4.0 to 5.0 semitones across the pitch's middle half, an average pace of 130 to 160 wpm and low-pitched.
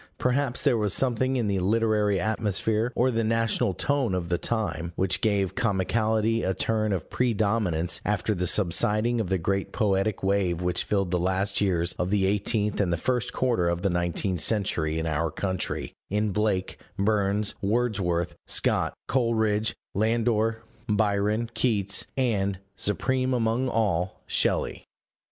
No: average, 3.3 semitones; average, 150 wpm; low, 105 Hz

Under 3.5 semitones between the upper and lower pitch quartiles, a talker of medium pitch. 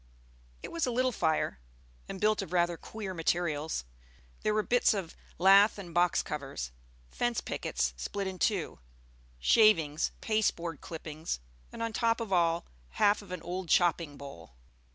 No: average, 4.7 semitones; medium, 180 Hz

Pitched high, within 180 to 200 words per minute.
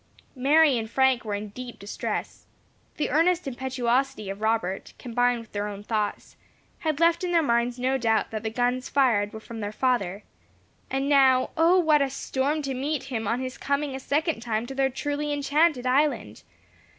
Yes: very high, 255 Hz; average, 185 wpm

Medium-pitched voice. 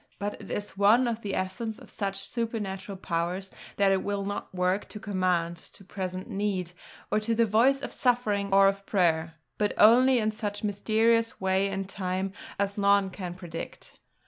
No: high, 200 Hz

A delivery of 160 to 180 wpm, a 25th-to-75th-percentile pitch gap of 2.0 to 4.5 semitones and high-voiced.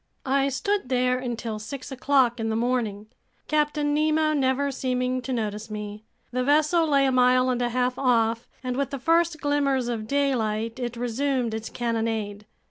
Yes: average, 170 wpm; average, 3.4 semitones; very high, 255 Hz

